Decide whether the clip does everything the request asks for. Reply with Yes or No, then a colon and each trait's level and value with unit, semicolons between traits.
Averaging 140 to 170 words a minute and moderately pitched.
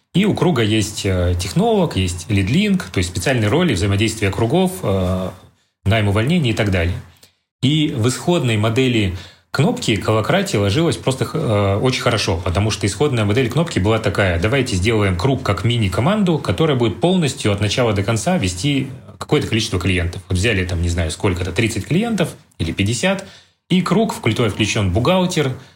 No: average, 155 wpm; low, 115 Hz